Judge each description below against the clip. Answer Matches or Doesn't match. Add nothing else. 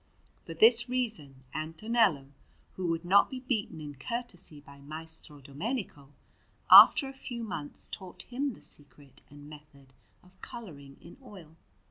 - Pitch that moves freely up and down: Matches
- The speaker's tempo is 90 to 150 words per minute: Matches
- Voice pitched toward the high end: Doesn't match